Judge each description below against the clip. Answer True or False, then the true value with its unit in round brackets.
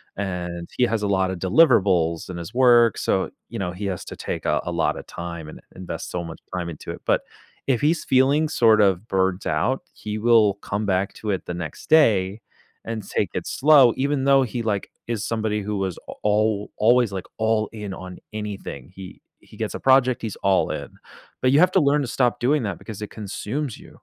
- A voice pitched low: True (105 Hz)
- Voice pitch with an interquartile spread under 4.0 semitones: False (4.7 semitones)